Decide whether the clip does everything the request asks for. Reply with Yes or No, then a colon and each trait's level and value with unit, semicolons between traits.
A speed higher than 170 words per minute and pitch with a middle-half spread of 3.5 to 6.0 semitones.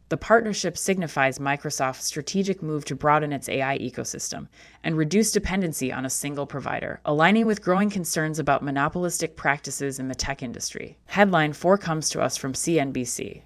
No: average, 160 wpm; average, 4.4 semitones